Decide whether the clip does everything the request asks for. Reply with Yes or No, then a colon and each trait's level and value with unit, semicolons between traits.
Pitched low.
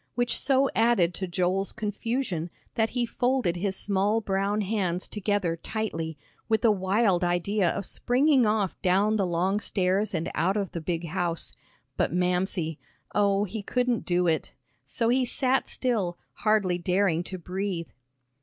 No: high, 195 Hz